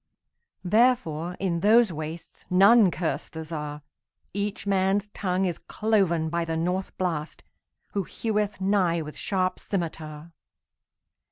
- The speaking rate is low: Yes, slow, 100 wpm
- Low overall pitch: No, medium, 180 Hz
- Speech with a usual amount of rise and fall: Yes, average, 3.7 semitones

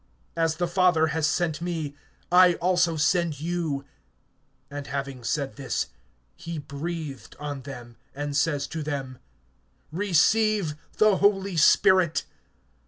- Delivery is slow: Yes, slow, 120 wpm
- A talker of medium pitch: Yes, medium, 160 Hz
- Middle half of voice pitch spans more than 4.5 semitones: No, average, 3.6 semitones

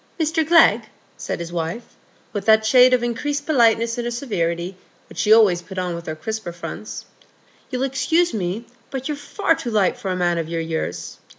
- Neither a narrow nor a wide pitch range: No, wide, 6.7 semitones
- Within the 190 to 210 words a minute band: Yes, average, 195 wpm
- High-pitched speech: Yes, high, 220 Hz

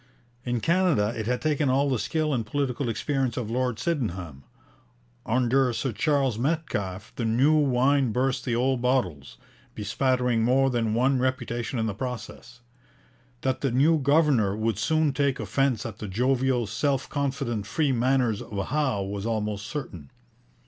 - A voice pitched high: No, low, 125 Hz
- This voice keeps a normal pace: Yes, average, 155 wpm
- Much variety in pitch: No, average, 3.5 semitones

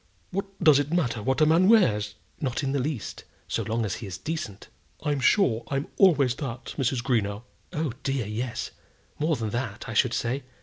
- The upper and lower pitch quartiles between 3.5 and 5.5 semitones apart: Yes, average, 5.1 semitones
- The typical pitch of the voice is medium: No, low, 130 Hz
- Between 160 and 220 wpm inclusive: Yes, average, 190 wpm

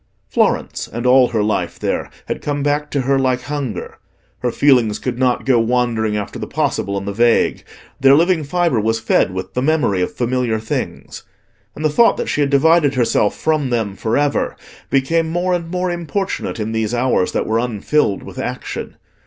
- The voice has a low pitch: Yes, low, 130 Hz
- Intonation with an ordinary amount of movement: Yes, average, 4.8 semitones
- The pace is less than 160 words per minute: No, average, 190 wpm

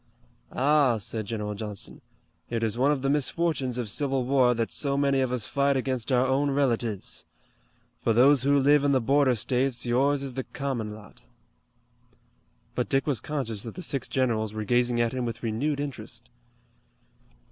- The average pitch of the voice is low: Yes, low, 130 Hz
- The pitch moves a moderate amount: Yes, average, 3.3 semitones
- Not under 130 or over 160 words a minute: No, average, 175 wpm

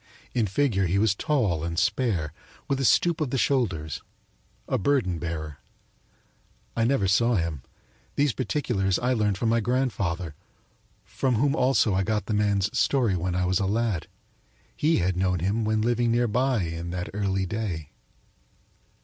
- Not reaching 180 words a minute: Yes, average, 165 wpm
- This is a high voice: No, low, 105 Hz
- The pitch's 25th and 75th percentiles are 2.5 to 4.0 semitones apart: No, average, 5.1 semitones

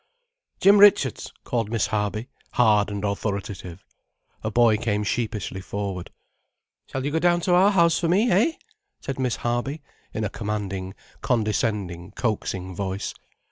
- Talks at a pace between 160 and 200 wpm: No, average, 140 wpm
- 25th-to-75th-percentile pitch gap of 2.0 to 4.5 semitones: No, average, 5.1 semitones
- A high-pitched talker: No, low, 110 Hz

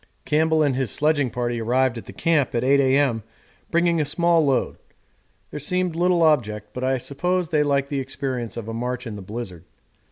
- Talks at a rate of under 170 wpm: No, average, 195 wpm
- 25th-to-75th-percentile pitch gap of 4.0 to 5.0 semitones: Yes, average, 4.6 semitones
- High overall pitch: No, low, 135 Hz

